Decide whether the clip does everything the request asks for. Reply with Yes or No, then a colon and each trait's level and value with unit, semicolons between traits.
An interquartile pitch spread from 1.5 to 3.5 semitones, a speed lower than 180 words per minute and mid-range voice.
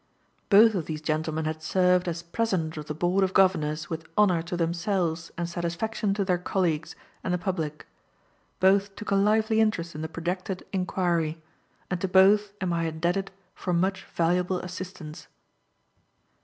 Yes: average, 2.7 semitones; average, 160 wpm; medium, 180 Hz